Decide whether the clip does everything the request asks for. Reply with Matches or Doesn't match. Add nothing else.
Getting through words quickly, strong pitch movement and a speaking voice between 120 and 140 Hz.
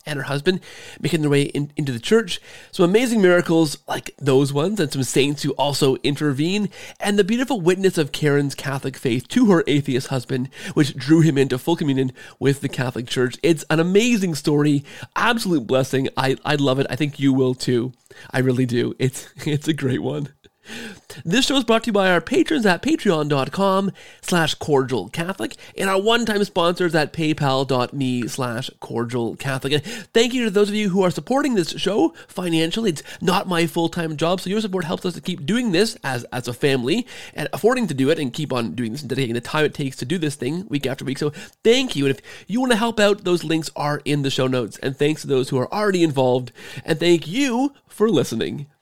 Doesn't match